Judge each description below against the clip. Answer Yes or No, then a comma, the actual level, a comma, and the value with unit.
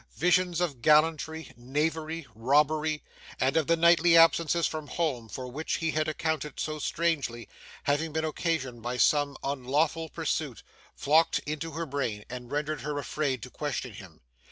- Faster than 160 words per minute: No, average, 155 wpm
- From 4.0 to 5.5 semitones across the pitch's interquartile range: No, average, 3.3 semitones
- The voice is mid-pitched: Yes, medium, 150 Hz